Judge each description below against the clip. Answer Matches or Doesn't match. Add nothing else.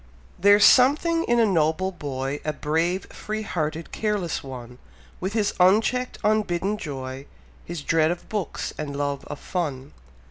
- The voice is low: Doesn't match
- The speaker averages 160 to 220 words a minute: Doesn't match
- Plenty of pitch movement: Matches